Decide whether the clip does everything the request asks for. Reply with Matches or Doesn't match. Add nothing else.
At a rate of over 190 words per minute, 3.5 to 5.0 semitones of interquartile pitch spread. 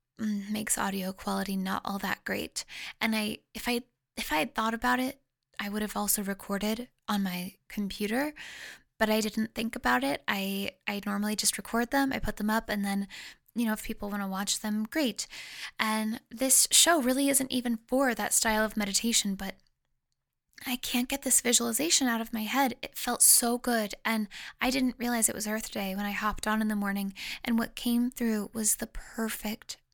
Doesn't match